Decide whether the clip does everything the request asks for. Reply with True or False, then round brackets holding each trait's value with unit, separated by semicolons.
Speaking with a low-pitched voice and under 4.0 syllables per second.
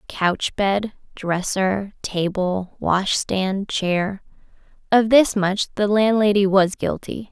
False (195 Hz; 3.1 syllables/s)